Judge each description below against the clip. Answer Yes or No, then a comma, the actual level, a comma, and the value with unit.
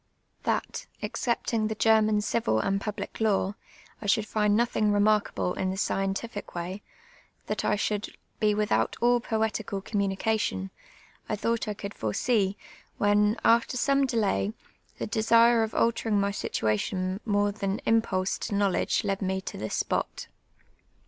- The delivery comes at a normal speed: Yes, average, 145 wpm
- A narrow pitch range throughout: Yes, narrow, 2.2 semitones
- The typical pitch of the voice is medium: No, high, 210 Hz